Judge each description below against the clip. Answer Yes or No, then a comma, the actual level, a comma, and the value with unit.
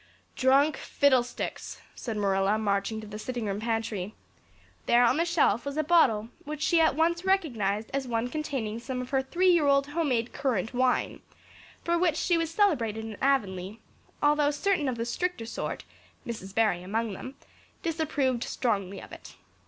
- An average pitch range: No, wide, 5.7 semitones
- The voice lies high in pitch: Yes, very high, 250 Hz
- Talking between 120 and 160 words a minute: No, average, 170 wpm